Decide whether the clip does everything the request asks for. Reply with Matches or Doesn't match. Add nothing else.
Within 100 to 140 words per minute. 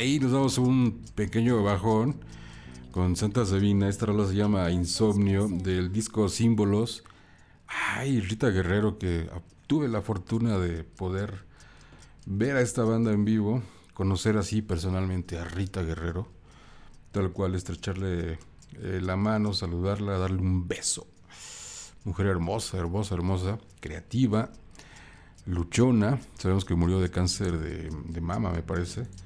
Matches